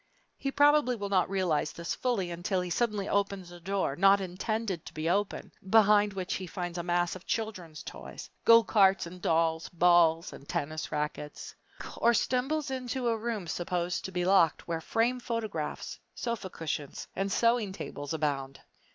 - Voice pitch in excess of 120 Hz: Yes, high, 190 Hz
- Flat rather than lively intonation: No, average, 4.6 semitones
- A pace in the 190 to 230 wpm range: No, average, 170 wpm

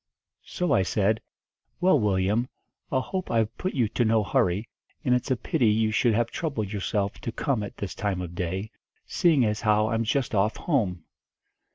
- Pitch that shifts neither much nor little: Yes, average, 3.5 semitones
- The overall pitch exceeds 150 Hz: No, low, 110 Hz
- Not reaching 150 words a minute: No, average, 185 wpm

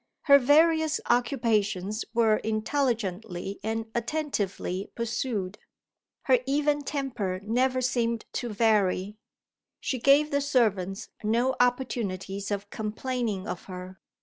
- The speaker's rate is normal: No, slow, 105 wpm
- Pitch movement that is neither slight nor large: Yes, average, 4.4 semitones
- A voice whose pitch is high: Yes, high, 230 Hz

